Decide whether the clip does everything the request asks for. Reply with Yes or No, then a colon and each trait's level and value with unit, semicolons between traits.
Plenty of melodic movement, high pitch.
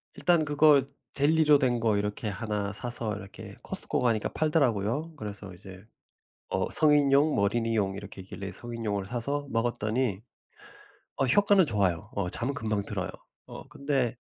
No: wide, 5.8 semitones; low, 115 Hz